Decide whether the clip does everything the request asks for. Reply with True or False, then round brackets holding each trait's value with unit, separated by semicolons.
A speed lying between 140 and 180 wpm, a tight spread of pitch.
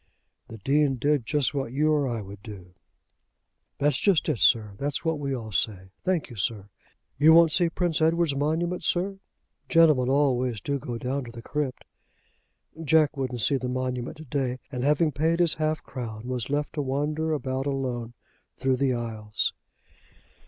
False (175 wpm; 4.0 semitones)